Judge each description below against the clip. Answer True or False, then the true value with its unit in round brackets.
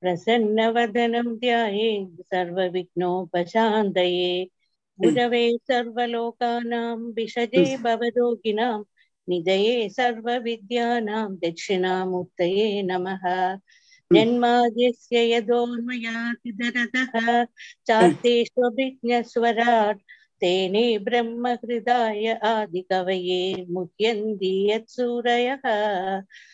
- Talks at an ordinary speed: False (60 wpm)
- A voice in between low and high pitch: False (230 Hz)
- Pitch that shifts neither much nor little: True (4.0 semitones)